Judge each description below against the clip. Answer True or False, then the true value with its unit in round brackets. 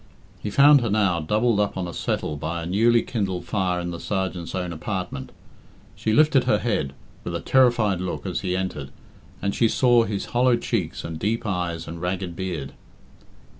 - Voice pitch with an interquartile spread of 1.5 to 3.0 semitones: False (4.8 semitones)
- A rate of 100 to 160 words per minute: False (185 wpm)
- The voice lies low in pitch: True (95 Hz)